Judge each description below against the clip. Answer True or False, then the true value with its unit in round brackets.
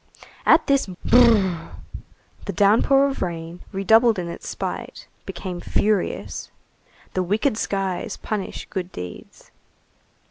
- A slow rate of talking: True (110 wpm)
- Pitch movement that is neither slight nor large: True (3.8 semitones)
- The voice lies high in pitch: True (195 Hz)